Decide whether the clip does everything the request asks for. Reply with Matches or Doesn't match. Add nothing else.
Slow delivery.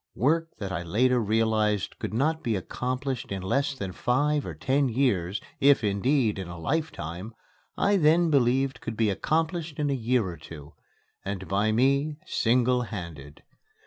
Doesn't match